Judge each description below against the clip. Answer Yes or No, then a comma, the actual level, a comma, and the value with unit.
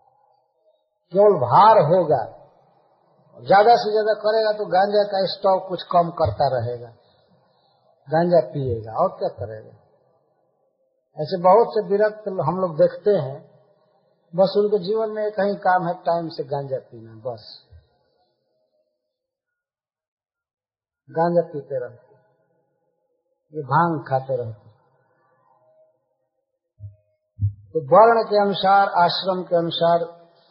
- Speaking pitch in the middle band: Yes, medium, 180 Hz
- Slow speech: Yes, slow, 105 wpm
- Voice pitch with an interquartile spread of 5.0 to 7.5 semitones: Yes, wide, 5.6 semitones